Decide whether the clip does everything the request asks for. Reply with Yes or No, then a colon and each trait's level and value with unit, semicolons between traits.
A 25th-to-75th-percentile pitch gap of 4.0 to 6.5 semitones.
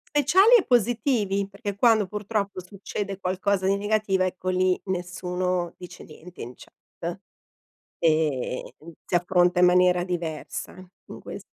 No: narrow, 2.4 semitones